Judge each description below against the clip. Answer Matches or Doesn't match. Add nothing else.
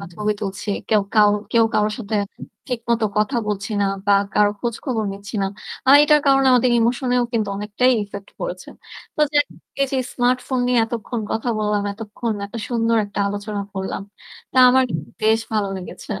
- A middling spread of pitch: Matches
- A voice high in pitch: Matches